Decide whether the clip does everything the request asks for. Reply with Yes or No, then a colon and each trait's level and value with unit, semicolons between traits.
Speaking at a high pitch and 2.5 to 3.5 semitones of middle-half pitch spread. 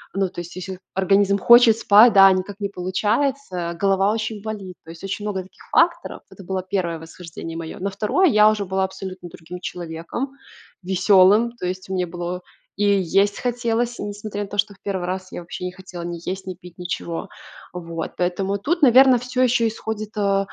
Yes: high, 195 Hz; average, 2.9 semitones